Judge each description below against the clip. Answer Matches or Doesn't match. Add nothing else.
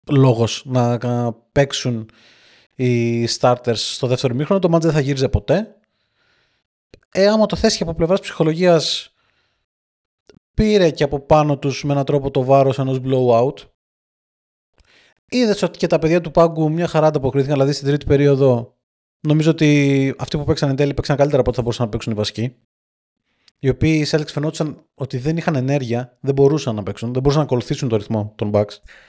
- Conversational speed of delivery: Doesn't match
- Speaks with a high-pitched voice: Doesn't match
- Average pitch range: Matches